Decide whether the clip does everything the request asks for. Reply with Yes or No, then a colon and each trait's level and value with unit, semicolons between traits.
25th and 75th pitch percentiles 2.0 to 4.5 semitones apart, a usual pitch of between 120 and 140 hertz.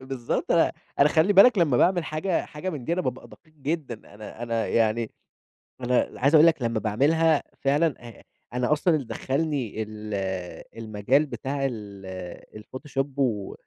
No: wide, 5.5 semitones; low, 135 Hz